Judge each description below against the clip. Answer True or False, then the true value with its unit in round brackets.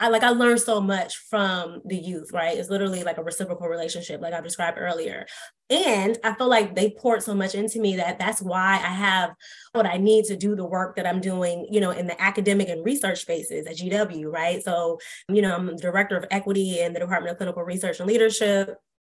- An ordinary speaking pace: False (225 wpm)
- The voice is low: False (190 Hz)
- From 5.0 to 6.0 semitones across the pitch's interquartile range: False (3.2 semitones)